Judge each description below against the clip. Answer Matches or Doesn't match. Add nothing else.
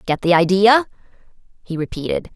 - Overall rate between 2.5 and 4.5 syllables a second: Doesn't match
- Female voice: Matches